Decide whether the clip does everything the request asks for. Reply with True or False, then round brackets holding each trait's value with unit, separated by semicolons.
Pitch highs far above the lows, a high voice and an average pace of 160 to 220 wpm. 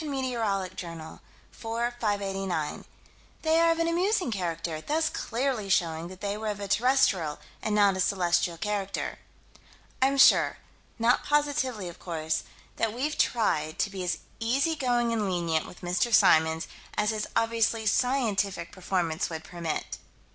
False (5.8 semitones; 205 Hz; 145 wpm)